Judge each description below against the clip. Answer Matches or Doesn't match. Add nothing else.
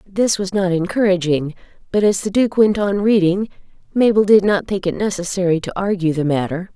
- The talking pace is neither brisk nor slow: Matches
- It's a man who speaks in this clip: Doesn't match